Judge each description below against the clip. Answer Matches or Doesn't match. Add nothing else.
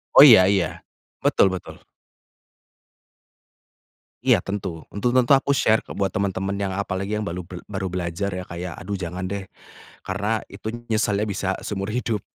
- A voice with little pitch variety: Matches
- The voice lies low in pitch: Matches